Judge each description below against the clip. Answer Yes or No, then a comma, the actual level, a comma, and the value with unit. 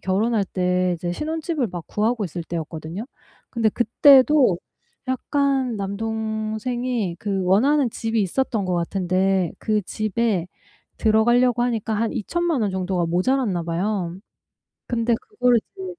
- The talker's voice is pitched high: Yes, high, 220 Hz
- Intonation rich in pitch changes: No, average, 5.0 semitones